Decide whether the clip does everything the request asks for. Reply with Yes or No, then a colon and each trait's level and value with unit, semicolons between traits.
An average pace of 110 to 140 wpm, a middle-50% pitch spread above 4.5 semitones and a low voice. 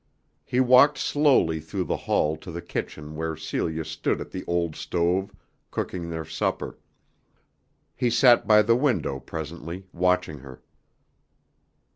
Yes: slow, 135 wpm; wide, 5.4 semitones; very low, 85 Hz